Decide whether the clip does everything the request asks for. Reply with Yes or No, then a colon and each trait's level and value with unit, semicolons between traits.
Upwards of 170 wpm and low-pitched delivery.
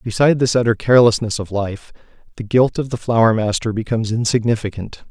No: average, 165 wpm; low, 115 Hz